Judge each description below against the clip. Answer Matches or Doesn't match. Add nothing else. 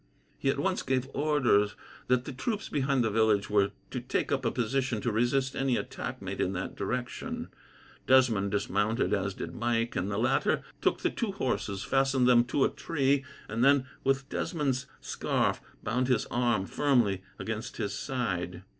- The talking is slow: Doesn't match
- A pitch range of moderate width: Matches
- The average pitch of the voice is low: Matches